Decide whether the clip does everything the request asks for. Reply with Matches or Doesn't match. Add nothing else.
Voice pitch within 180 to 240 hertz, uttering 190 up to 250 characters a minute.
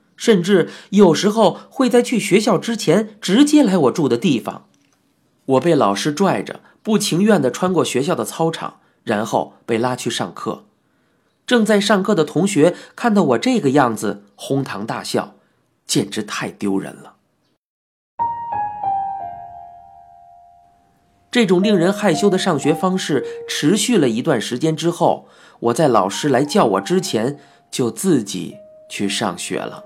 Matches